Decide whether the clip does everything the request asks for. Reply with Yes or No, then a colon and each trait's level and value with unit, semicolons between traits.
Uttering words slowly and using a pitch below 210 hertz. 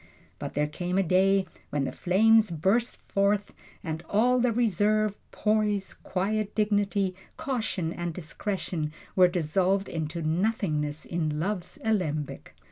Yes: slow, 125 wpm; high, 190 Hz